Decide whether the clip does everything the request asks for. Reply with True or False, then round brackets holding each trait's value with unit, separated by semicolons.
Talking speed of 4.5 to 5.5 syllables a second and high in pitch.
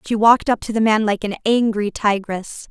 True (5.2 syllables/s; 215 Hz)